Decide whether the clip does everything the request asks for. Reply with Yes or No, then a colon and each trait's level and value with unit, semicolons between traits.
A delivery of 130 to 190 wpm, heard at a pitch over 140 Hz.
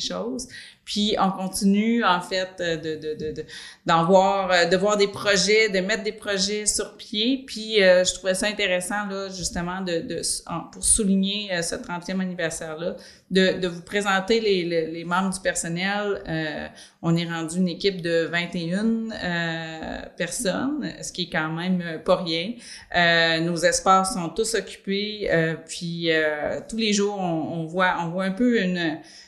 Yes: average, 170 wpm; medium, 185 Hz